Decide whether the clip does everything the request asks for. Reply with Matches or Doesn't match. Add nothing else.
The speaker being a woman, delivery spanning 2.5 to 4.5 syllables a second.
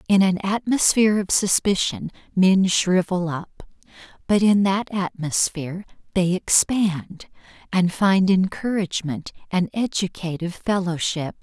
Matches